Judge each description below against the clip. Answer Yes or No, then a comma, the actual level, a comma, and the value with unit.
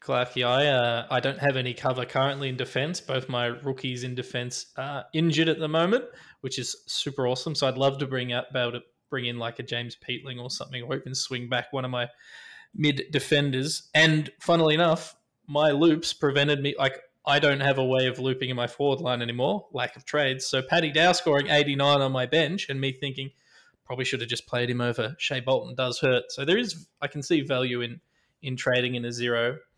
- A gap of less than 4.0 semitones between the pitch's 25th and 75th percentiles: Yes, average, 2.8 semitones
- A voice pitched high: No, low, 130 Hz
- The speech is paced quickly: Yes, fast, 225 wpm